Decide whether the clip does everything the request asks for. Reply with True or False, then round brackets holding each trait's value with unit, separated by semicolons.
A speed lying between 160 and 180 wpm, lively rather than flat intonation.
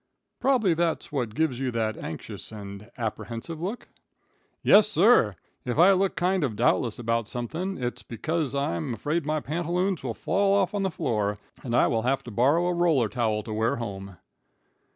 True (175 wpm; 7.2 semitones)